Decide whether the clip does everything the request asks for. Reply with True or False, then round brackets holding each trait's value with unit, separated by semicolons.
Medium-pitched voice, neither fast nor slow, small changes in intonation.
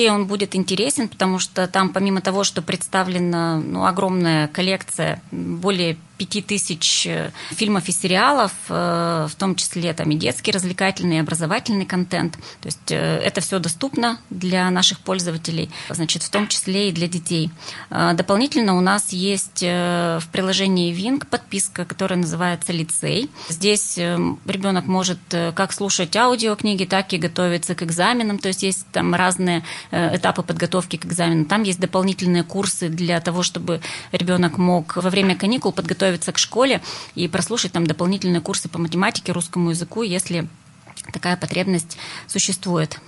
True (180 Hz; 140 wpm; 2.2 semitones)